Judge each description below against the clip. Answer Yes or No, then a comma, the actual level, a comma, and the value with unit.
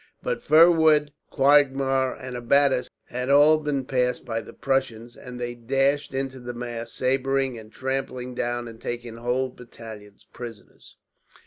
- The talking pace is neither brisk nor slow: Yes, average, 145 wpm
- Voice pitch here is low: Yes, low, 130 Hz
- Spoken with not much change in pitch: Yes, narrow, 2.2 semitones